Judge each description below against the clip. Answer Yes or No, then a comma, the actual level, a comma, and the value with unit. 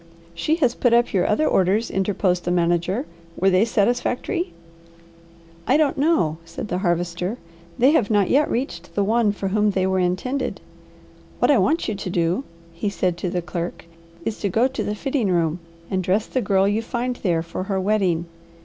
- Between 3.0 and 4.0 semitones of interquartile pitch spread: No, average, 4.9 semitones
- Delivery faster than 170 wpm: Yes, average, 190 wpm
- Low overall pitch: No, high, 195 Hz